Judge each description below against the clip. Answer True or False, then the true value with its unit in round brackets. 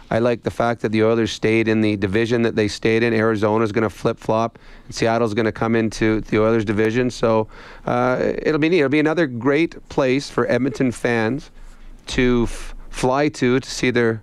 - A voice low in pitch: True (115 Hz)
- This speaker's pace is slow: False (205 wpm)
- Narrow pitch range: True (2.2 semitones)